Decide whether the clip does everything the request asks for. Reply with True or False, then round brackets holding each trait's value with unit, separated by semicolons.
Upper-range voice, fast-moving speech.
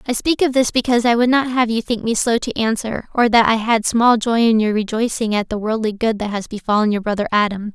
True (225 Hz; 265 wpm)